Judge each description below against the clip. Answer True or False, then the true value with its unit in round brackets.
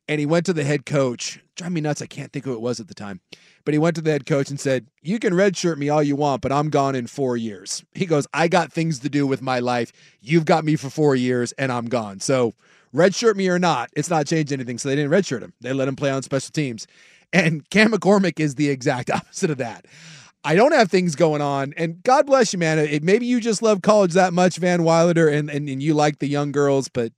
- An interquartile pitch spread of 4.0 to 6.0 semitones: True (4.4 semitones)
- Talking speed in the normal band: False (265 wpm)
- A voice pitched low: False (150 Hz)